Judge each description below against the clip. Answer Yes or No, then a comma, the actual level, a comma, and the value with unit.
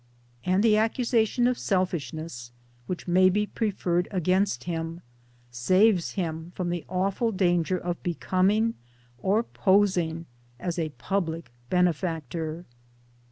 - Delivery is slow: Yes, slow, 115 wpm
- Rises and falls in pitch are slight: No, average, 3.1 semitones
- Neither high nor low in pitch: Yes, medium, 180 Hz